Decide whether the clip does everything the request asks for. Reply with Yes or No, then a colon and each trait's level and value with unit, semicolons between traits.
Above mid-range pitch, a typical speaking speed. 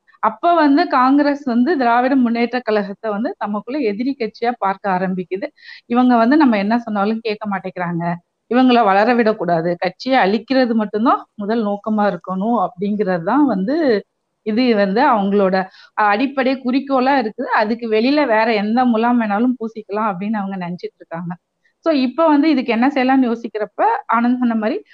No: high, 230 Hz; fast, 140 wpm